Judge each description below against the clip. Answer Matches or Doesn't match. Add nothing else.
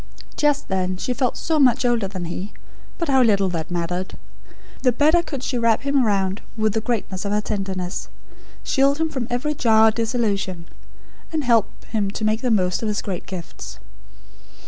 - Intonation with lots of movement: Doesn't match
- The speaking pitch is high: Matches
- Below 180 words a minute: Doesn't match